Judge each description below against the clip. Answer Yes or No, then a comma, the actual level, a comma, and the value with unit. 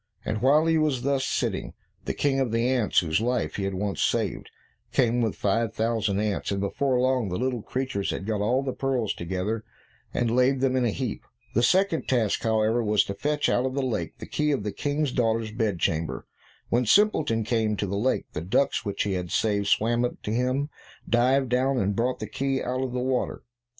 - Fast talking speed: Yes, fast, 215 wpm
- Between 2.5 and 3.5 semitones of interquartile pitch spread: No, average, 3.9 semitones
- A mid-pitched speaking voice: No, low, 120 Hz